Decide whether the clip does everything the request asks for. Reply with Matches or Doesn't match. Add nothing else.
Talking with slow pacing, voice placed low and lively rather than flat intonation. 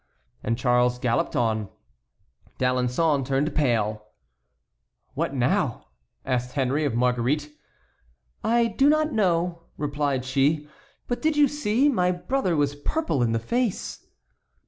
Doesn't match